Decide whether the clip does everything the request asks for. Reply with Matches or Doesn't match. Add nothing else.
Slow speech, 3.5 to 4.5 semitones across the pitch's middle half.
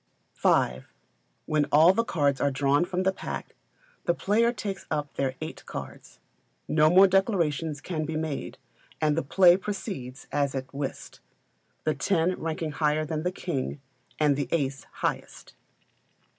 Doesn't match